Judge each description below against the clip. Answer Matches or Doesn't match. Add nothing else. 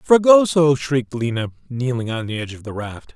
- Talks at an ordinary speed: Matches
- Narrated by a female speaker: Doesn't match